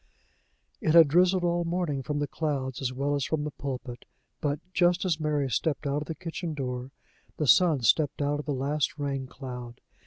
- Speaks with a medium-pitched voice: Yes, medium, 145 Hz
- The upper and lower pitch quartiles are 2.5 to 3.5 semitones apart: Yes, average, 3.1 semitones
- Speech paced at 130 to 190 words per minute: No, fast, 205 wpm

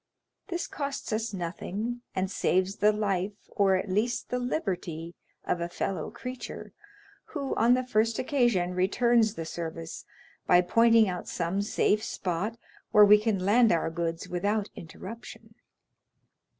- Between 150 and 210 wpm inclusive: No, average, 140 wpm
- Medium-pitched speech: No, high, 205 Hz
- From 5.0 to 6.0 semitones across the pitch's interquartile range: No, average, 4.3 semitones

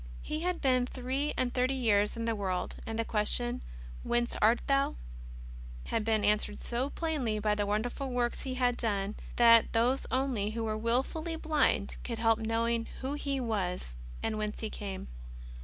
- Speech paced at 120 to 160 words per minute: No, average, 180 wpm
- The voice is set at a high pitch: Yes, high, 230 Hz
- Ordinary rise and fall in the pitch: Yes, average, 3.3 semitones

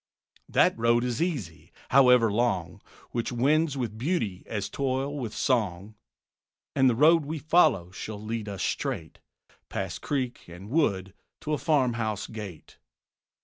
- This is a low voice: Yes, low, 120 Hz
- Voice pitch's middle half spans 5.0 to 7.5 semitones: Yes, average, 5.3 semitones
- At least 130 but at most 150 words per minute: Yes, average, 140 wpm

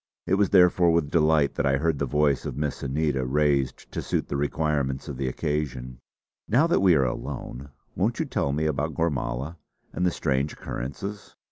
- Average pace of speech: Yes, average, 190 wpm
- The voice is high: No, very low, 75 Hz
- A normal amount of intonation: Yes, average, 3.2 semitones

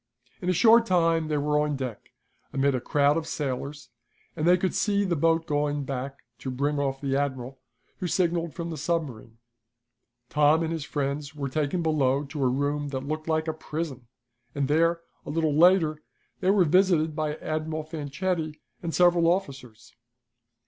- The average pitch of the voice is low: No, medium, 150 Hz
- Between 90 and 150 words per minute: No, average, 175 wpm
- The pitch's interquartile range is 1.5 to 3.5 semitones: Yes, average, 3.0 semitones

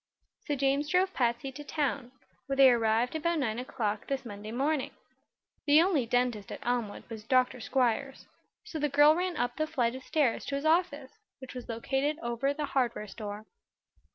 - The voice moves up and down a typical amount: Yes, average, 3.7 semitones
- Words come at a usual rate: Yes, average, 180 wpm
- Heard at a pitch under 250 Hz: No, very high, 265 Hz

